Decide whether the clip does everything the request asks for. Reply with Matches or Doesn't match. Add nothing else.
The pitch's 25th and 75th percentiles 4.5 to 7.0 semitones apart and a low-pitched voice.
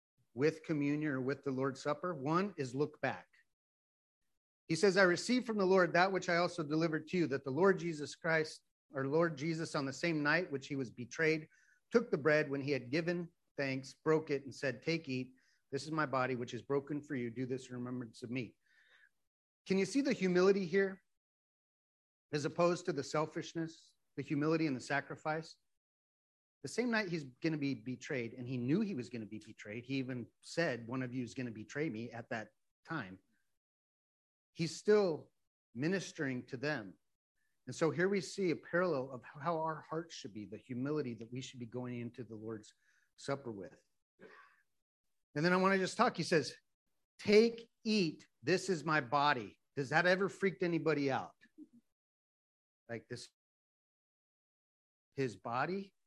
Doesn't match